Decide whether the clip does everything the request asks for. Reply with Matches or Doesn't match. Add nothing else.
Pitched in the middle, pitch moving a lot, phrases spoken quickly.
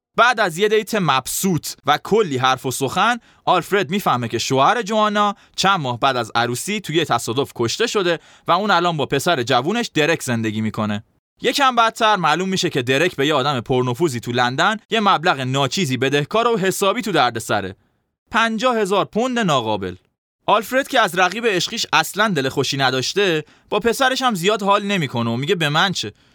Matches